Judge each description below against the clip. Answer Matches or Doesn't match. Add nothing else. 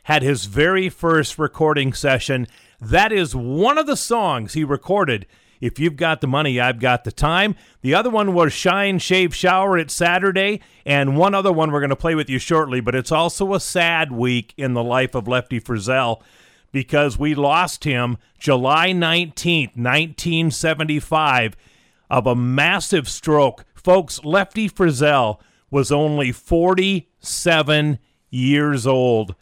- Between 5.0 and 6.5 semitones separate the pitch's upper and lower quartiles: Matches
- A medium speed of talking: Matches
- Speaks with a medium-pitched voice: Matches